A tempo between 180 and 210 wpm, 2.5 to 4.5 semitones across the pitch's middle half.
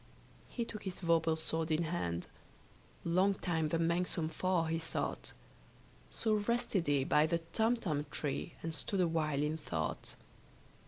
No: average, 145 wpm; average, 2.8 semitones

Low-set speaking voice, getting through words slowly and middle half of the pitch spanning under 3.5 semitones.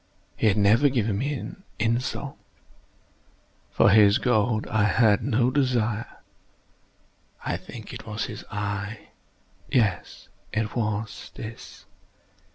Yes: low, 110 Hz; slow, 110 wpm; narrow, 2.5 semitones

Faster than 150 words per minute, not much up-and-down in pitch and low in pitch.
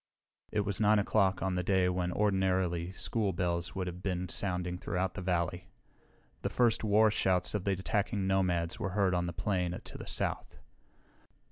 Yes: average, 175 wpm; narrow, 2.0 semitones; very low, 95 Hz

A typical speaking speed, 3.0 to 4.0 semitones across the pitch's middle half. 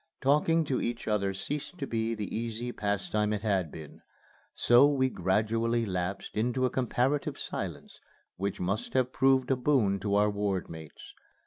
No: average, 160 wpm; average, 4.5 semitones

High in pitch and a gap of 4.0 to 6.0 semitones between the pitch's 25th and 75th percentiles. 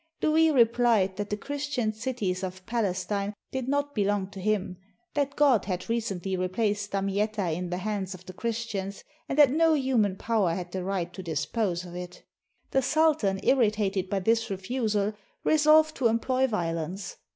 Yes: high, 205 Hz; average, 4.7 semitones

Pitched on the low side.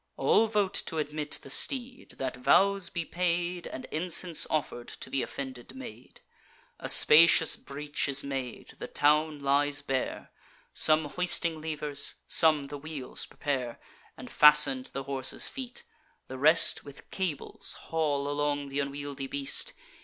No: medium, 145 Hz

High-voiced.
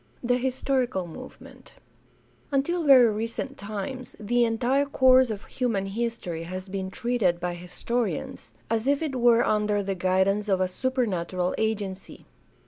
Yes: high, 220 Hz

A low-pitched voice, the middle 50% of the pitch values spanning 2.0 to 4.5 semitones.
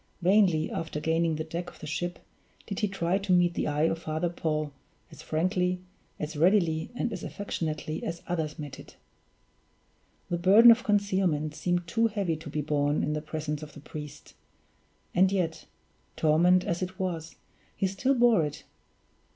No: medium, 170 Hz; average, 3.3 semitones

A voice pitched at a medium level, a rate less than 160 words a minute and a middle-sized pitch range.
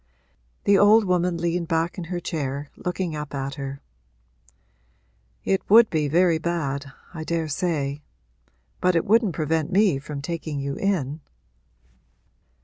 Yes: medium, 165 Hz; slow, 135 wpm; average, 3.9 semitones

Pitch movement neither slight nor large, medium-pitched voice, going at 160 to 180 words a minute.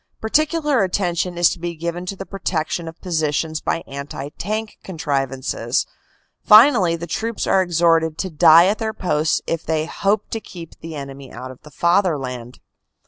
Yes: average, 4.0 semitones; medium, 170 Hz; average, 170 wpm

